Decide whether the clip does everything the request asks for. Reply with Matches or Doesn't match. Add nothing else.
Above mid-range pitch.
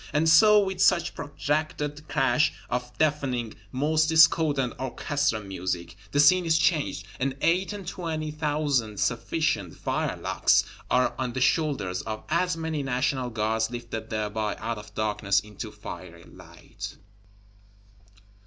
Doesn't match